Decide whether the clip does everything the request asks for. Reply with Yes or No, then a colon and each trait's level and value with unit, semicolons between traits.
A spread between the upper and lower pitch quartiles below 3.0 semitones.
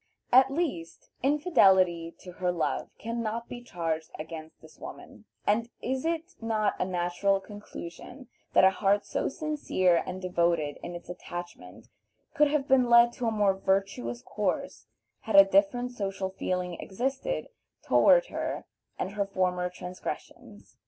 No: wide, 5.4 semitones